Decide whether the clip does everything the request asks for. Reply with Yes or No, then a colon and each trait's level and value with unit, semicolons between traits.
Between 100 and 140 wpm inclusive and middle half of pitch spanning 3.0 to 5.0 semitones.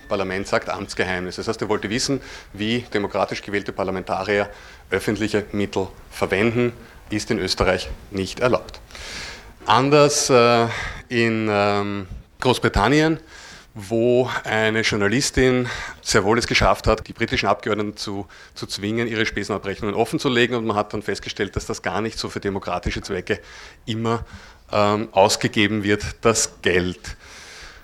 No: average, 130 wpm; narrow, 2.6 semitones